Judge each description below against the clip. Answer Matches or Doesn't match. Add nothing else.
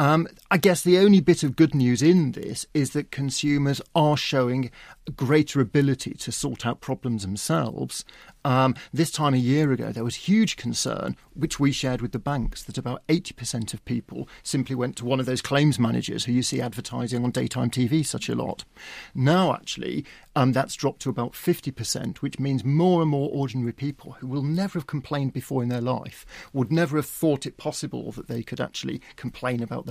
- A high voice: Doesn't match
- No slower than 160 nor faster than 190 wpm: Doesn't match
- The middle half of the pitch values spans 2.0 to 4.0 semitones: Matches